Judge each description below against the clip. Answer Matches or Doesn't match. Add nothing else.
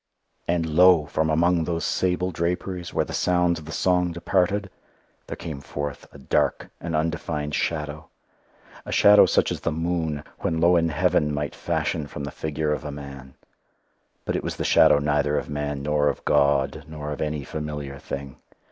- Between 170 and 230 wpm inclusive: Matches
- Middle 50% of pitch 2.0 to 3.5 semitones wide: Matches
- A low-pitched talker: Matches